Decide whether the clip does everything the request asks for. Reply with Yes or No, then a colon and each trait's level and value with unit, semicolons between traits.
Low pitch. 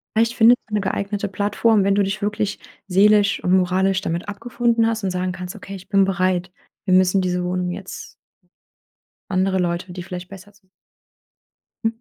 No: high, 195 Hz